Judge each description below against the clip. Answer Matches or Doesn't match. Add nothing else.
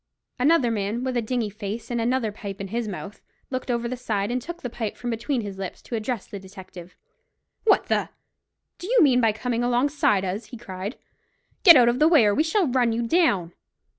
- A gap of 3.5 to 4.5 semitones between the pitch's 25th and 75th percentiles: Matches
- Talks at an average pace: Doesn't match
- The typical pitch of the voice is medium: Doesn't match